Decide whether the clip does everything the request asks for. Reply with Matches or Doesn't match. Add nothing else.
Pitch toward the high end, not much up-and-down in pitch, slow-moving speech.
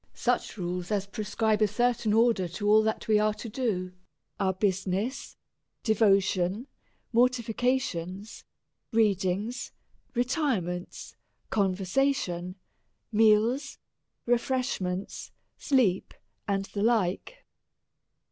Doesn't match